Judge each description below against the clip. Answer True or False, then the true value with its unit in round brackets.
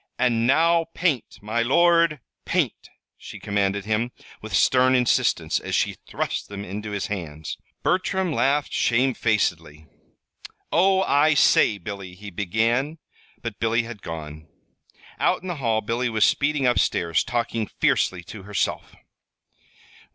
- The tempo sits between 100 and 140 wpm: True (135 wpm)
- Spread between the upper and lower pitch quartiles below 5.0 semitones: False (5.5 semitones)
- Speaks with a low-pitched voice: True (115 Hz)